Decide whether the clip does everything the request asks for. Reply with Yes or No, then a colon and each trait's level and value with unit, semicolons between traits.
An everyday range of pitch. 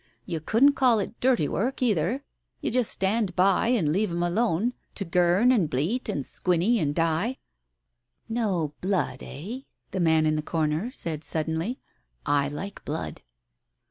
No: wide, 6.3 semitones